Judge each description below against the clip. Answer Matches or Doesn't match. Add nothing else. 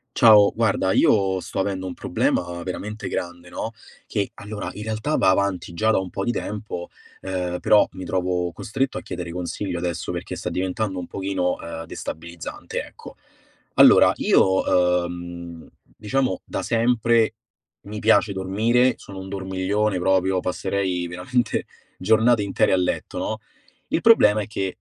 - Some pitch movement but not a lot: Matches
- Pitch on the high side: Doesn't match